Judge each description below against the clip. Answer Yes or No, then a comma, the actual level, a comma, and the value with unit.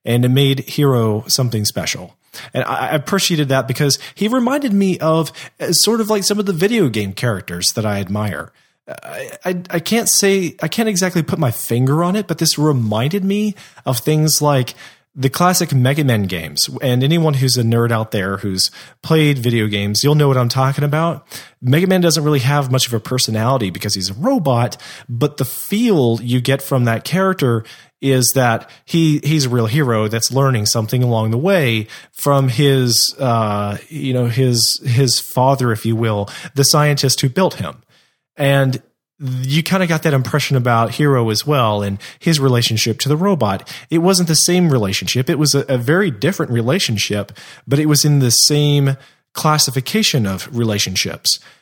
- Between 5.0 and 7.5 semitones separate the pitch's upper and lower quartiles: Yes, average, 5.3 semitones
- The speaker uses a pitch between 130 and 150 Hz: Yes, low, 135 Hz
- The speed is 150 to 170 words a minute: No, average, 180 wpm